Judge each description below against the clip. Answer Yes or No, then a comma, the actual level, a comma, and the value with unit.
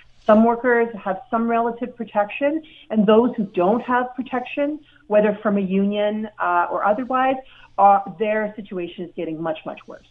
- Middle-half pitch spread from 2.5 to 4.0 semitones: Yes, average, 3.7 semitones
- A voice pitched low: No, high, 215 Hz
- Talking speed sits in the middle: Yes, average, 160 wpm